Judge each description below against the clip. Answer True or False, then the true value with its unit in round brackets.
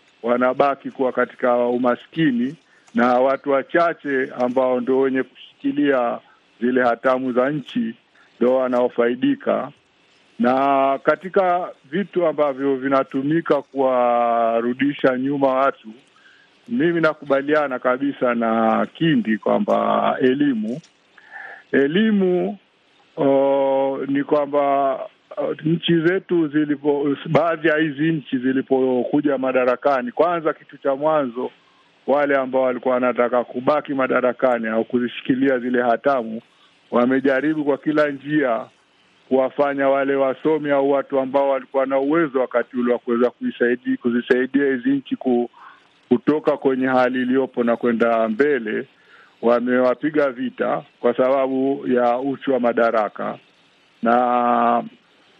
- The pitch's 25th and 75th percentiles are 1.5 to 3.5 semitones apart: True (3.2 semitones)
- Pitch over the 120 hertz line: True (135 Hz)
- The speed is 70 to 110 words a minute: True (105 wpm)